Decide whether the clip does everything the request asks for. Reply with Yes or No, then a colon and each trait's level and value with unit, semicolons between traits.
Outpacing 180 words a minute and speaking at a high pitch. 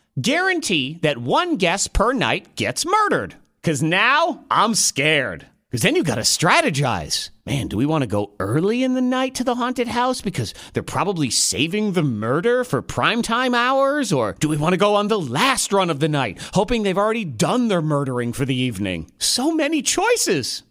Yes: average, 190 wpm; high, 200 Hz